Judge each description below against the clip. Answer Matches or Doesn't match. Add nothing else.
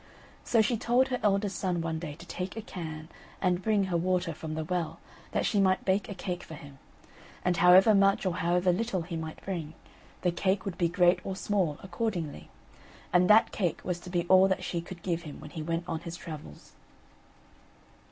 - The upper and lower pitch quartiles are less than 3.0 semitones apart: Matches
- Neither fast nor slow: Doesn't match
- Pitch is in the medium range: Matches